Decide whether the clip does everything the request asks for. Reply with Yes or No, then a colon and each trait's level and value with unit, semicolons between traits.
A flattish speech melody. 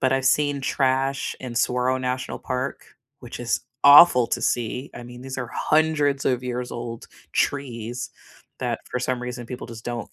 Yes: narrow, 1.7 semitones